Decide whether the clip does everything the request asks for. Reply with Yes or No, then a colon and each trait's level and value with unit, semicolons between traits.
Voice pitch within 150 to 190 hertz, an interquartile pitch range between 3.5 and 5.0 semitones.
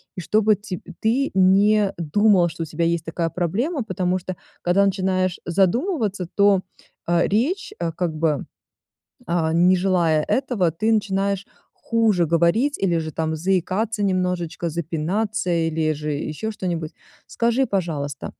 Yes: medium, 185 Hz; average, 3.8 semitones